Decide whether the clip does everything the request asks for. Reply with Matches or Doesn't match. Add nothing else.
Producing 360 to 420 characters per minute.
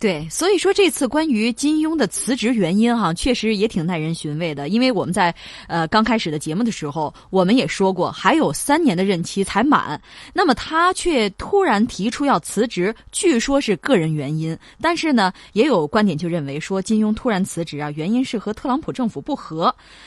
Doesn't match